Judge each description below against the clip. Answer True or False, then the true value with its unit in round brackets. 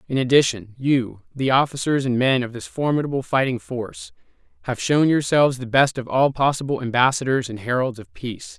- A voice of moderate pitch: False (130 Hz)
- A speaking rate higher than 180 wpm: False (175 wpm)